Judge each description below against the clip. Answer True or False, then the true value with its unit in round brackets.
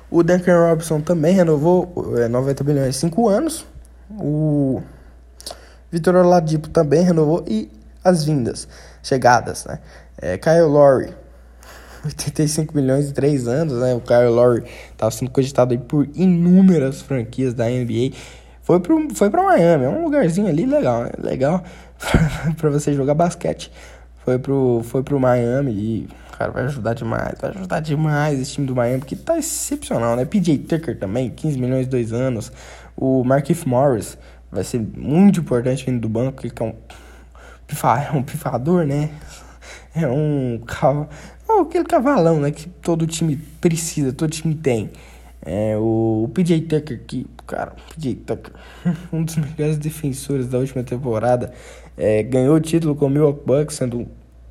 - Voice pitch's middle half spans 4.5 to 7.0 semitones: True (5.1 semitones)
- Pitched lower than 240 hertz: True (140 Hz)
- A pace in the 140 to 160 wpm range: True (155 wpm)